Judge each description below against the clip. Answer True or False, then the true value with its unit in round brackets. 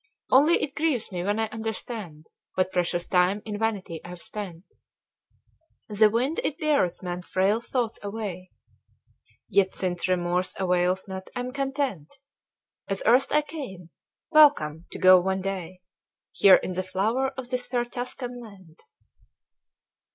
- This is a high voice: True (200 Hz)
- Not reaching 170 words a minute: True (140 wpm)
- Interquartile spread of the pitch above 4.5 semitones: True (5.2 semitones)